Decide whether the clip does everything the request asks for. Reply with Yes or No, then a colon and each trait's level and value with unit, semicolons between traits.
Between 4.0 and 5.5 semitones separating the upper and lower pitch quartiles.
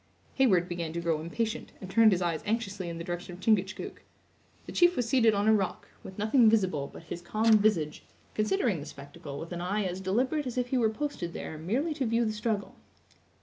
Yes: average, 4.6 semitones